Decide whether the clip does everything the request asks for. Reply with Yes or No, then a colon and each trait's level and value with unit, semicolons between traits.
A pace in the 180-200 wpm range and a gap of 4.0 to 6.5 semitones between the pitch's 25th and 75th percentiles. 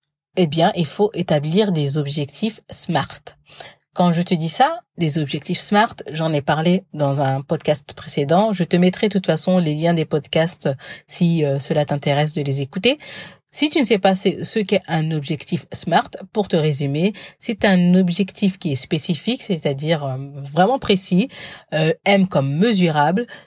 No: average, 165 wpm; average, 4.5 semitones